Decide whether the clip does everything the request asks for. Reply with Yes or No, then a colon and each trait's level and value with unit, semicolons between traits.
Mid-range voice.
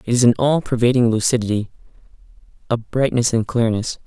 No: low, 120 Hz